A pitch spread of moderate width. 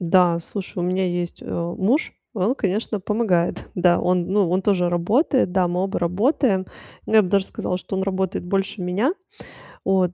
No: narrow, 2.3 semitones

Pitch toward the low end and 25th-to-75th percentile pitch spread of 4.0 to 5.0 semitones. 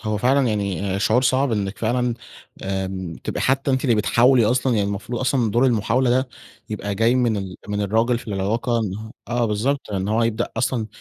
No: low, 115 Hz; average, 3.4 semitones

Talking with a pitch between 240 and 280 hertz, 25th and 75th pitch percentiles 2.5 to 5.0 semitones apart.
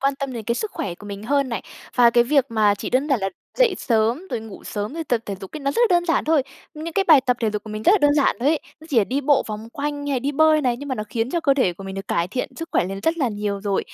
No: very high, 255 Hz; wide, 5.5 semitones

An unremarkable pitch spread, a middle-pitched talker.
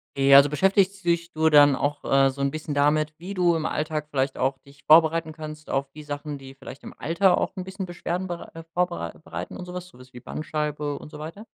Yes: average, 3.4 semitones; medium, 155 Hz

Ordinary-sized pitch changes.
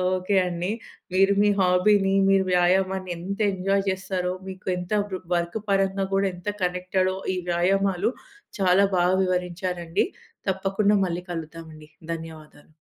No: narrow, 1.7 semitones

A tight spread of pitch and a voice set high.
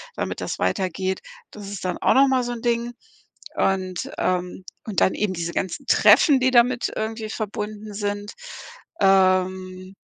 No: average, 3.5 semitones; high, 205 Hz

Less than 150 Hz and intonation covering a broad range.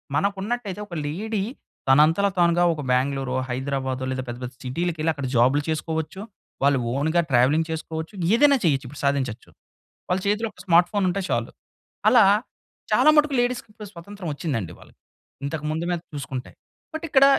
No: medium, 160 Hz; wide, 6.5 semitones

